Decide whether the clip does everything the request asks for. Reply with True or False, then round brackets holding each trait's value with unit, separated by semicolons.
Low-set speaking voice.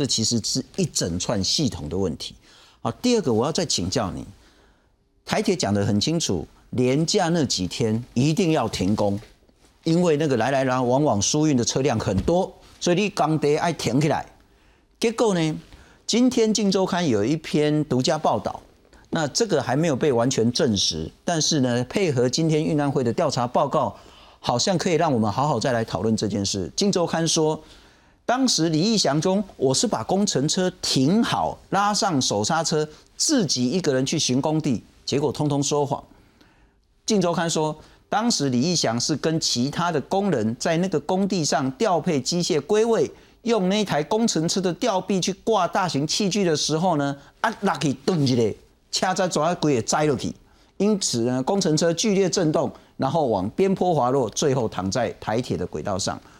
False (155 Hz)